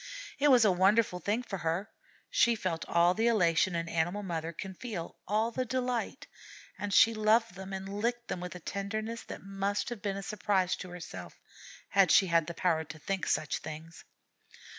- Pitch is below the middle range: No, high, 195 Hz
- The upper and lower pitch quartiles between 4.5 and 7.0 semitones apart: No, average, 3.9 semitones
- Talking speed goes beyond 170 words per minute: Yes, average, 195 wpm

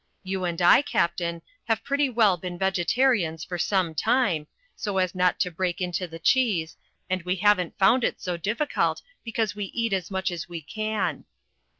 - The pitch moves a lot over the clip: No, average, 3.8 semitones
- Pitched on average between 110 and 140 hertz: No, medium, 185 Hz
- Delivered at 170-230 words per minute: Yes, average, 180 wpm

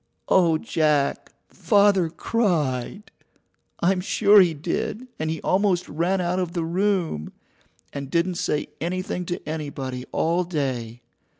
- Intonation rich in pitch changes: No, average, 3.7 semitones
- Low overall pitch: No, medium, 170 Hz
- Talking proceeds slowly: Yes, slow, 125 wpm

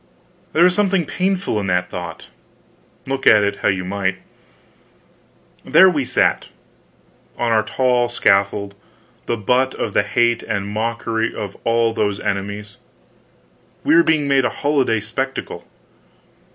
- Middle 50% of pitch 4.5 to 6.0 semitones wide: Yes, average, 4.9 semitones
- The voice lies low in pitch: Yes, low, 115 Hz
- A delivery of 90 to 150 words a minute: Yes, average, 140 wpm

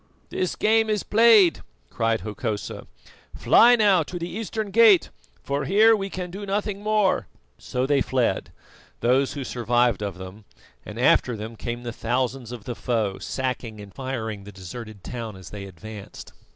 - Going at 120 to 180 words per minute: Yes, average, 165 wpm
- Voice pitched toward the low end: Yes, low, 125 Hz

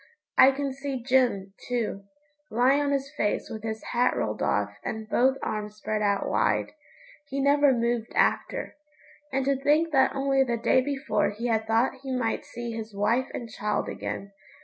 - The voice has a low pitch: No, high, 245 Hz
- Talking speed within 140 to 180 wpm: Yes, average, 175 wpm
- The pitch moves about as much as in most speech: Yes, average, 3.7 semitones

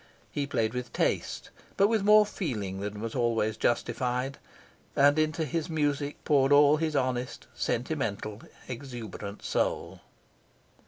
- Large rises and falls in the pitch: No, average, 4.7 semitones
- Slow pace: Yes, slow, 125 wpm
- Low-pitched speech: Yes, low, 130 Hz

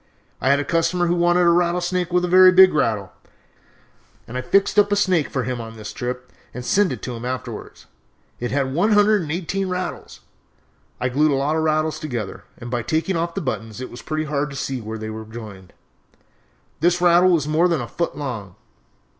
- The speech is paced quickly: Yes, fast, 215 wpm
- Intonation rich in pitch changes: Yes, wide, 6.1 semitones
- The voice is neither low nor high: Yes, medium, 155 Hz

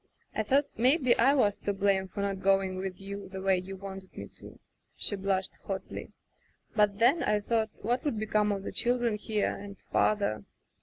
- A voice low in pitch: No, high, 200 Hz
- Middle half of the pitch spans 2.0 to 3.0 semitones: Yes, narrow, 2.4 semitones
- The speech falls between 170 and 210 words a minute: Yes, average, 190 wpm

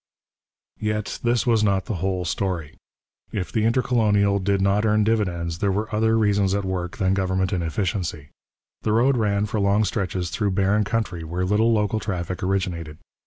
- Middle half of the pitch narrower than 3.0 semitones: Yes, narrow, 2.6 semitones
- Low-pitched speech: Yes, low, 100 Hz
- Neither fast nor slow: Yes, average, 165 wpm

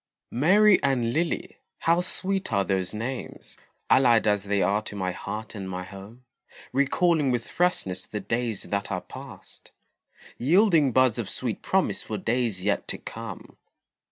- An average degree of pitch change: No, wide, 5.8 semitones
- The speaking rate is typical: Yes, average, 155 wpm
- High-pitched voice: No, low, 115 Hz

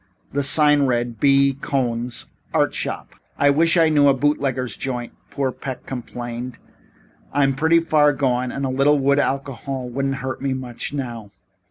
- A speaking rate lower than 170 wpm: Yes, average, 160 wpm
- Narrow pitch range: Yes, narrow, 2.3 semitones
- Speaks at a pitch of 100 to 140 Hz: Yes, low, 135 Hz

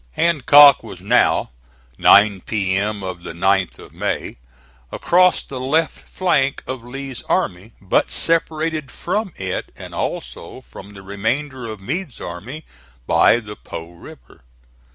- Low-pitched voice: Yes, low, 115 Hz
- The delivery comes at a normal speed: No, slow, 130 wpm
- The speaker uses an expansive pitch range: Yes, wide, 7.2 semitones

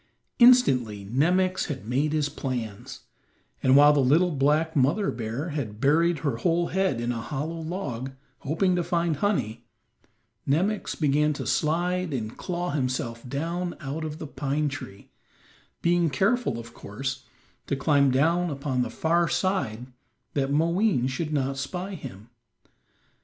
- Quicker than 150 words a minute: No, average, 145 wpm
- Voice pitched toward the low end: No, medium, 145 Hz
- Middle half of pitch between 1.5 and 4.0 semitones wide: No, average, 4.9 semitones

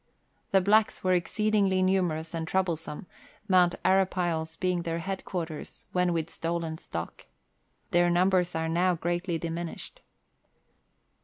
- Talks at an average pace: No, slow, 130 wpm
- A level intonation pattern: Yes, narrow, 2.1 semitones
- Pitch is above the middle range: No, medium, 175 Hz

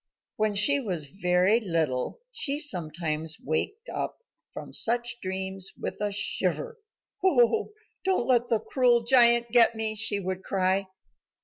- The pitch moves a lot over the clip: No, average, 4.5 semitones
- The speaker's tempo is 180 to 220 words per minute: No, slow, 135 wpm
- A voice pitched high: Yes, high, 215 Hz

